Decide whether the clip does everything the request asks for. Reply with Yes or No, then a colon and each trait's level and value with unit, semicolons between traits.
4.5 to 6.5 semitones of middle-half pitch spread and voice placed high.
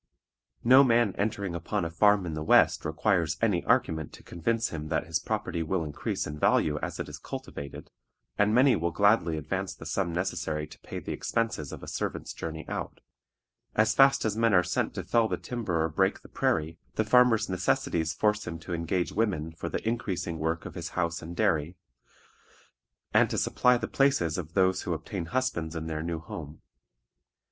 No: average, 5.1 semitones; very low, 85 Hz